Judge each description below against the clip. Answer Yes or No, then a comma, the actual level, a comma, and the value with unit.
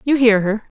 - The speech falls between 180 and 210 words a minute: No, fast, 225 wpm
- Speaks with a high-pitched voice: Yes, high, 230 Hz